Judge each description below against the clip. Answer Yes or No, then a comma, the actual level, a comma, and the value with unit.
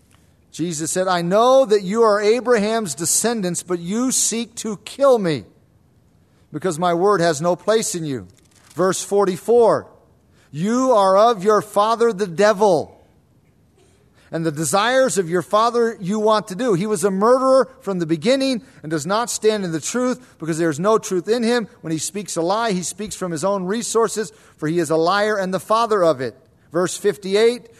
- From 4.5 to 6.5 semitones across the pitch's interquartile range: Yes, average, 4.8 semitones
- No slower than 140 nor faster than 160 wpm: No, average, 185 wpm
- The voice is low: No, high, 200 Hz